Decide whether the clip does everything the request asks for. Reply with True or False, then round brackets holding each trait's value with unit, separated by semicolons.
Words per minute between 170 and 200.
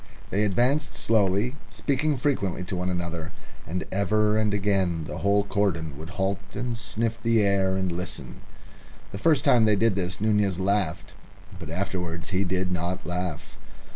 False (160 wpm)